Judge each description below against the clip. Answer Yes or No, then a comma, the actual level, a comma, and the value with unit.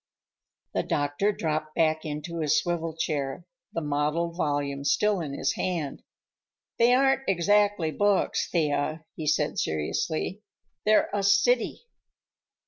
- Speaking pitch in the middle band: Yes, medium, 160 Hz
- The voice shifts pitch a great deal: No, average, 4.9 semitones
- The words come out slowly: Yes, slow, 125 wpm